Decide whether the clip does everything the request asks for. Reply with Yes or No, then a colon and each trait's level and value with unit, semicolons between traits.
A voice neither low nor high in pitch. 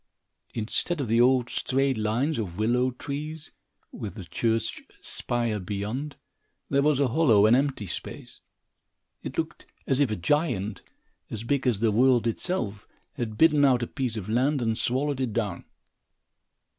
No: low, 120 Hz